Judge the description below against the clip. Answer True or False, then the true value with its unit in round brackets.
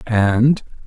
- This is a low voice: True (120 Hz)